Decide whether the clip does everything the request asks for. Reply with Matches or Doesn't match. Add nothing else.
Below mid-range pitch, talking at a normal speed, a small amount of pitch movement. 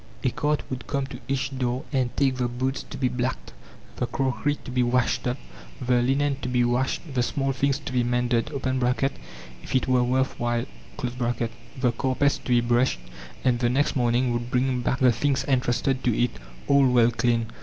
Matches